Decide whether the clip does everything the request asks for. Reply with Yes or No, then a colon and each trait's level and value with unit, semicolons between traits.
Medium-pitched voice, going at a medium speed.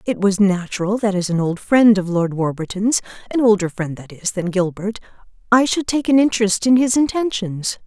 No: high, 205 Hz; average, 185 wpm